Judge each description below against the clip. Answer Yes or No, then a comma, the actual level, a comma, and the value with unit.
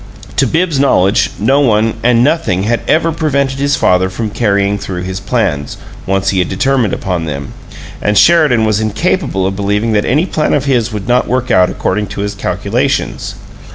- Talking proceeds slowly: No, average, 185 wpm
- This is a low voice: Yes, low, 110 Hz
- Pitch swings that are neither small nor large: No, wide, 5.9 semitones